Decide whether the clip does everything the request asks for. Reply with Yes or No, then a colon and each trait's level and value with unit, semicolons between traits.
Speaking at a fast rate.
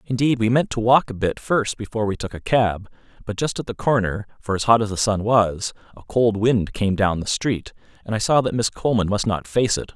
Yes: fast, 255 wpm